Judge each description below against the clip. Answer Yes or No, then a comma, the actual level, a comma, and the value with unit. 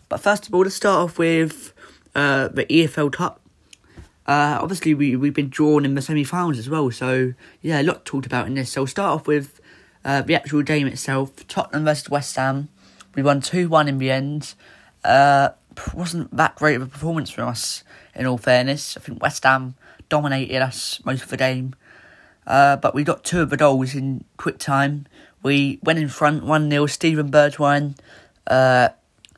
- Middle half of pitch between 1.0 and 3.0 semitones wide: Yes, narrow, 2.5 semitones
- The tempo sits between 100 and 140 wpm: No, average, 190 wpm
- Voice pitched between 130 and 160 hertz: Yes, medium, 140 Hz